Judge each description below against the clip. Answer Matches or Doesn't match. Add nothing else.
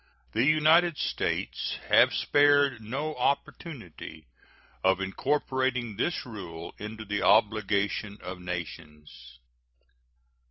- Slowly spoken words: Matches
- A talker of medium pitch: Doesn't match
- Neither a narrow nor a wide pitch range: Doesn't match